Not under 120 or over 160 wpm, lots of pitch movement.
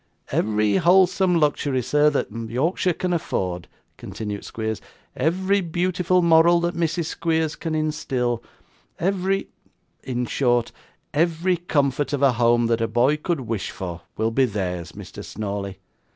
Yes: slow, 135 wpm; wide, 7.1 semitones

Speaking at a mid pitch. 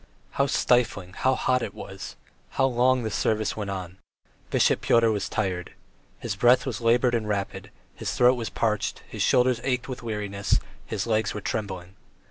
No: low, 110 Hz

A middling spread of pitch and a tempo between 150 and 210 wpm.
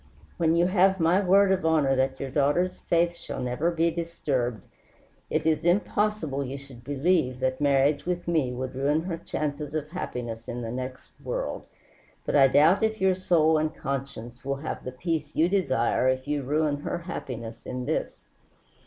Yes: average, 4.6 semitones; average, 180 wpm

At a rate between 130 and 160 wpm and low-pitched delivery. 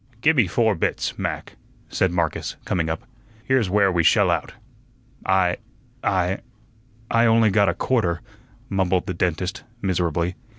Yes: average, 140 wpm; very low, 95 Hz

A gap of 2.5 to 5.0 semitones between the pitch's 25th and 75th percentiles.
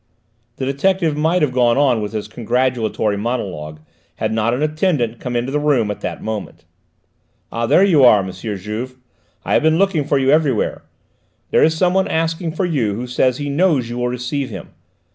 No: wide, 5.4 semitones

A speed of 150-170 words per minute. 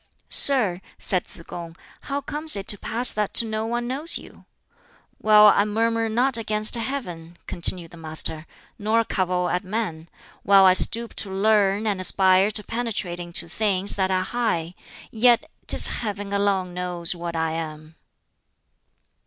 Yes: average, 155 wpm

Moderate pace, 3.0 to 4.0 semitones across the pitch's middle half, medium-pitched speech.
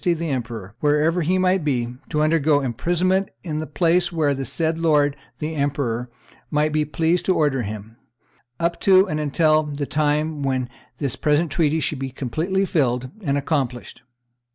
Yes: average, 165 wpm; average, 3.4 semitones; medium, 150 Hz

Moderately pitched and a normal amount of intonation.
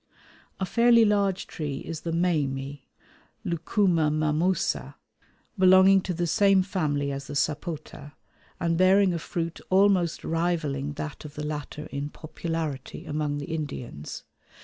Yes: medium, 165 Hz; average, 4.0 semitones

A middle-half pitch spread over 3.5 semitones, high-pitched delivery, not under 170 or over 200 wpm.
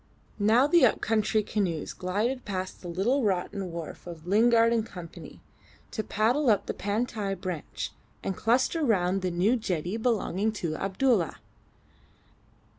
No: average, 4.1 semitones; high, 205 Hz; average, 140 wpm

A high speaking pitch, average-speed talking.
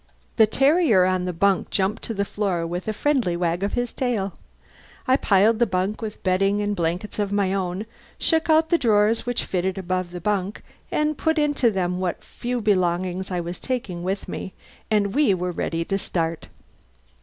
Yes: high, 195 Hz; average, 190 wpm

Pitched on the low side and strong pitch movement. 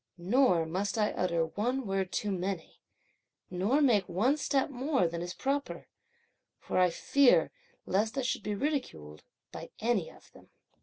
No: high, 205 Hz; wide, 6.5 semitones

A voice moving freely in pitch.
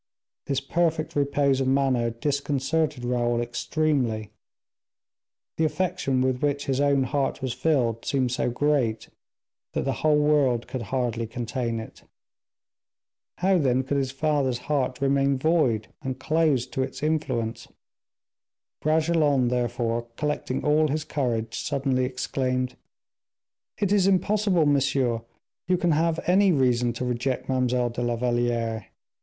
No: average, 3.5 semitones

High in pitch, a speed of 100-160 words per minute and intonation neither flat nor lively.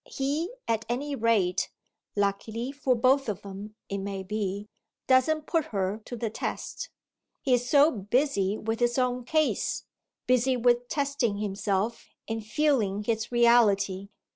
Yes: high, 230 Hz; average, 140 wpm; average, 4.3 semitones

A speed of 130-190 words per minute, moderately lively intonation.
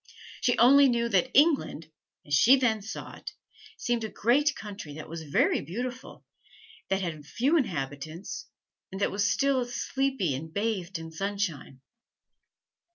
No: average, 150 wpm; wide, 7.4 semitones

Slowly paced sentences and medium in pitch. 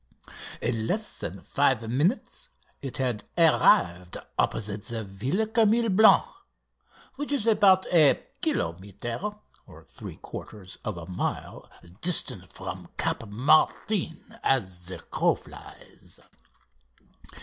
No: slow, 105 wpm; low, 130 Hz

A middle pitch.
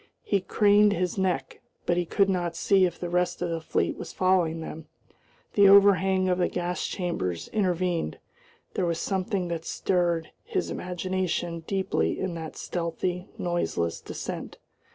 Yes: medium, 180 Hz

